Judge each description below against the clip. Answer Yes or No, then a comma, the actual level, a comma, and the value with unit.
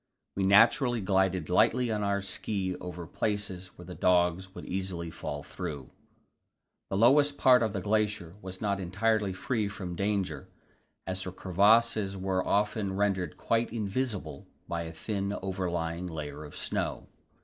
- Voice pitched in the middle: No, very low, 95 Hz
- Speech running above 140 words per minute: Yes, average, 150 wpm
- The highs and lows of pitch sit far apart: No, average, 2.8 semitones